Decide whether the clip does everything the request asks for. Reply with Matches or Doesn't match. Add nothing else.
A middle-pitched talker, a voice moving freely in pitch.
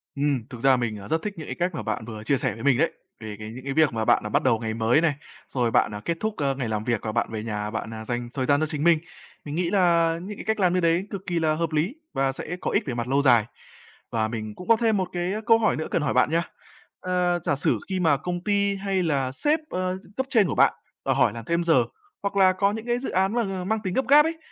Matches